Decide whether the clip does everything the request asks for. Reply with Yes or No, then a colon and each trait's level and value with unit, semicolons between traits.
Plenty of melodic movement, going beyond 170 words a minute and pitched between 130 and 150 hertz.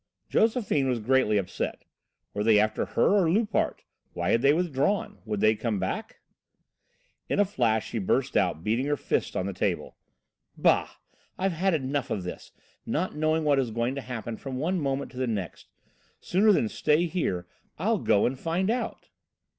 Yes: wide, 7.3 semitones; average, 180 wpm; low, 135 Hz